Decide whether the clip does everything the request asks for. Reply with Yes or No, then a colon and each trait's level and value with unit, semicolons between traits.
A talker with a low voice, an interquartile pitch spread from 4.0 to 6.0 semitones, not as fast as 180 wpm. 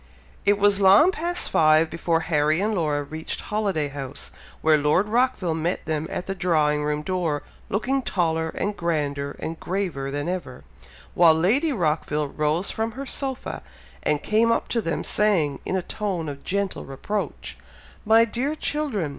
No: medium, 175 Hz; wide, 5.6 semitones; average, 165 wpm